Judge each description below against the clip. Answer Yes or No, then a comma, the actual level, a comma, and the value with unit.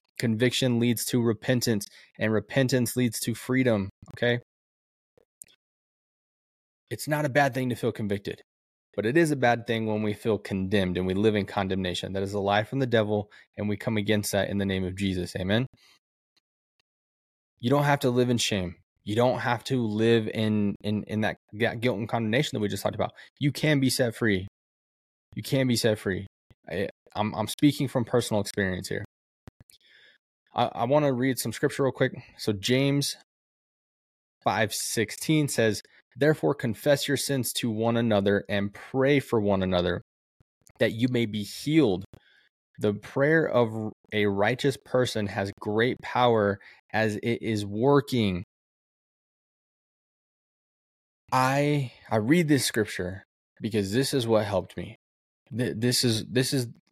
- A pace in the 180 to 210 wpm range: No, average, 160 wpm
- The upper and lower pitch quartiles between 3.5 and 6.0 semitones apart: Yes, average, 4.0 semitones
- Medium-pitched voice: No, low, 115 Hz